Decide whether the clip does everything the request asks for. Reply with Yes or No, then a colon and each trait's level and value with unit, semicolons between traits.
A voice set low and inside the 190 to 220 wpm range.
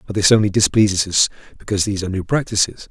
Yes: low, 100 Hz; fast, 205 wpm